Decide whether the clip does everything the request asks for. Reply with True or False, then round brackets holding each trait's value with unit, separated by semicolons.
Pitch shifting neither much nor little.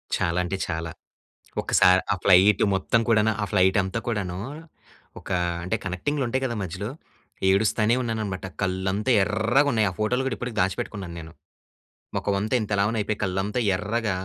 True (3.3 semitones)